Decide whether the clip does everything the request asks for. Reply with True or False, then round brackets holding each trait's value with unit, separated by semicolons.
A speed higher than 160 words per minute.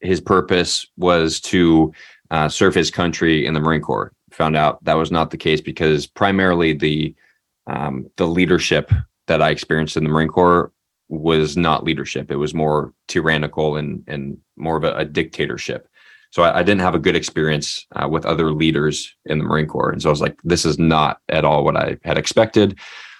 True (195 wpm)